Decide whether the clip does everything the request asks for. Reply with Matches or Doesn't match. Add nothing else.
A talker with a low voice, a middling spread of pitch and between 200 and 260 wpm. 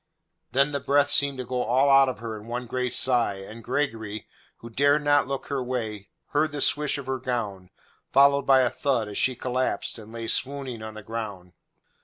Matches